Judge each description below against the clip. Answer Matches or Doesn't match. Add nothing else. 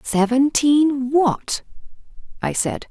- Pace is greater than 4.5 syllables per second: Doesn't match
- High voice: Matches